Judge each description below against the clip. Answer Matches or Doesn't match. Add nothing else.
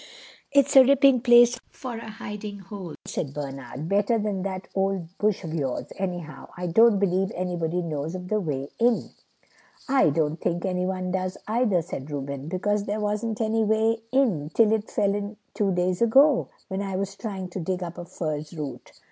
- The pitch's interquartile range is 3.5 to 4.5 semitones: Matches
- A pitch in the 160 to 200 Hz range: Matches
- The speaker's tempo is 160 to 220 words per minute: Matches